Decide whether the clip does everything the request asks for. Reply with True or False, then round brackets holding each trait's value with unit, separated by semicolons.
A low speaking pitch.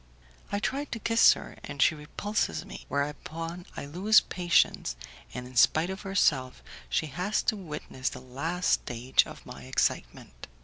False (155 Hz)